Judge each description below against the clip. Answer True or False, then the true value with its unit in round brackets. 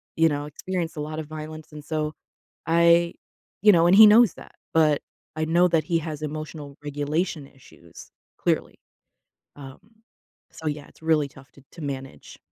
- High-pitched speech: False (155 Hz)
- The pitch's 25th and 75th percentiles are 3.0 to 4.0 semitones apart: False (2.5 semitones)